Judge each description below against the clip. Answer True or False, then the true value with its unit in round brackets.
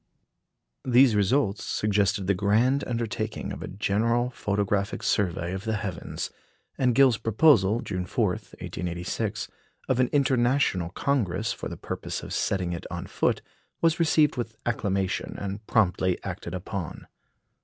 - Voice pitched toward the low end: True (105 Hz)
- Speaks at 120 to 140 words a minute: True (135 wpm)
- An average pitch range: True (4.2 semitones)